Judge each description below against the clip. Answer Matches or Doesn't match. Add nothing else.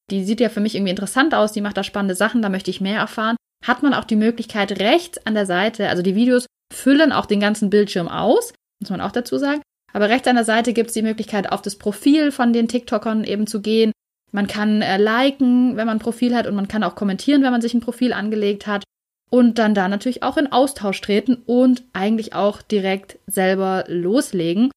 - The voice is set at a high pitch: Matches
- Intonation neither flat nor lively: Matches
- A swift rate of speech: Matches